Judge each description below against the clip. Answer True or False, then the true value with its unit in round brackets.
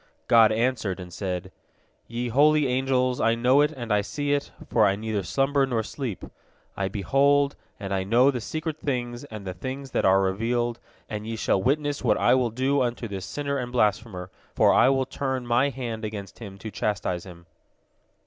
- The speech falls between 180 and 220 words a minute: True (190 wpm)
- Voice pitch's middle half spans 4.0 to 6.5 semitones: True (4.5 semitones)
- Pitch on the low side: True (120 Hz)